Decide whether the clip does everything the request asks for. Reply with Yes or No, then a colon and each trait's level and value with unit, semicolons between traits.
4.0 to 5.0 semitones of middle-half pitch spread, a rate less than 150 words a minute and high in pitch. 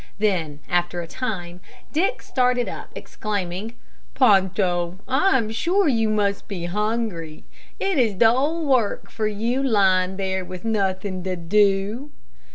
Yes: average, 4.4 semitones; slow, 135 wpm; high, 205 Hz